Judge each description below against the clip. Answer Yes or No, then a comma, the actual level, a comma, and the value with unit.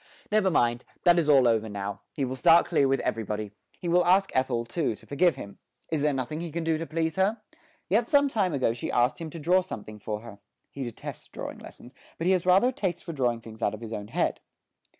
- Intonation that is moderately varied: No, wide, 7.0 semitones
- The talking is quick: Yes, fast, 245 wpm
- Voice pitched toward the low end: No, medium, 145 Hz